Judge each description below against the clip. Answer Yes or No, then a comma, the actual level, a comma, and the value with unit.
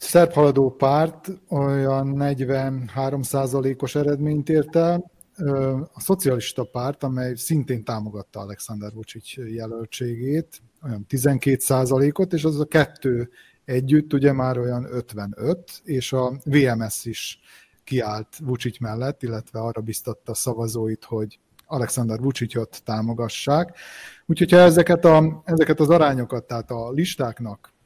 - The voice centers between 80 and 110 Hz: No, low, 135 Hz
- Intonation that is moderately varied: Yes, average, 4.2 semitones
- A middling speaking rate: Yes, average, 120 wpm